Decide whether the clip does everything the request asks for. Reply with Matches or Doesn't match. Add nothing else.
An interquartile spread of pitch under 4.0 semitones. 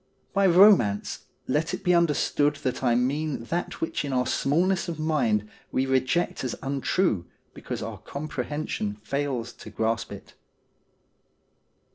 Doesn't match